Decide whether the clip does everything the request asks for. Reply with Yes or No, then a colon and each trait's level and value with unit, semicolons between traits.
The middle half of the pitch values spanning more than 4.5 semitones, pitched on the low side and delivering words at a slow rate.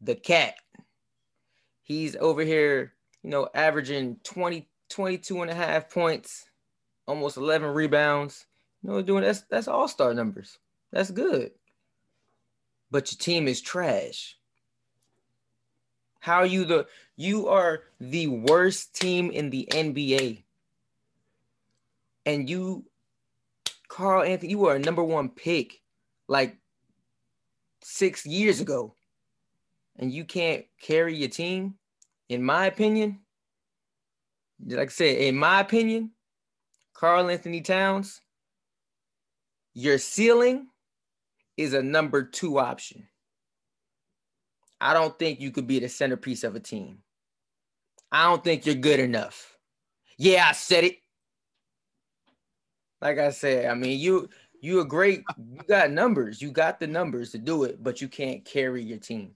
No: average, 5.3 semitones; medium, 155 Hz; slow, 130 wpm